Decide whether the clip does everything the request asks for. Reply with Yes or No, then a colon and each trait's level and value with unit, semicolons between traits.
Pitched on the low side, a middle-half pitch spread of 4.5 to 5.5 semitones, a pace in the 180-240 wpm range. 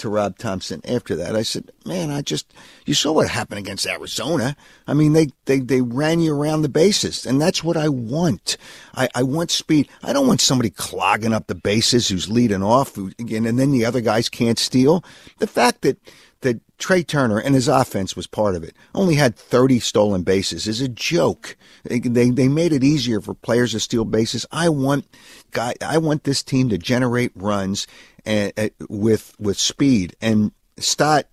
Yes: low, 120 Hz; average, 5.0 semitones; average, 200 wpm